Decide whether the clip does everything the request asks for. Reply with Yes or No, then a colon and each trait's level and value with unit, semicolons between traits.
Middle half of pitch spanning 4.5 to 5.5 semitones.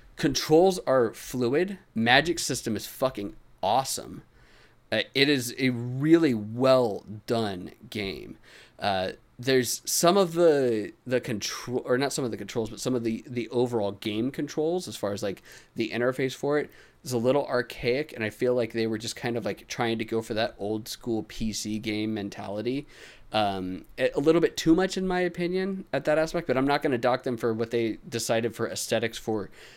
No: average, 3.8 semitones